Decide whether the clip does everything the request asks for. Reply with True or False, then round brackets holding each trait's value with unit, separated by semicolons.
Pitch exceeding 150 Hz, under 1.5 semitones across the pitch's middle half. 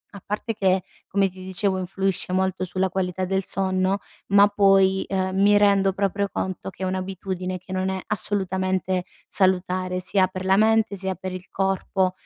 True (190 Hz; 0.8 semitones)